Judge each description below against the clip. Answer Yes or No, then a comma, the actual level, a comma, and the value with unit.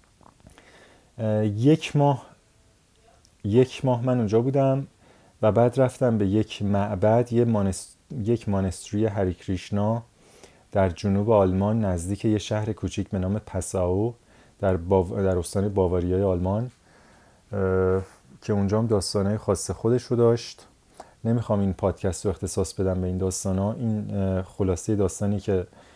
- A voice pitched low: Yes, low, 105 Hz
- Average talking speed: Yes, average, 130 wpm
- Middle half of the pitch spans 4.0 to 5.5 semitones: No, average, 3.0 semitones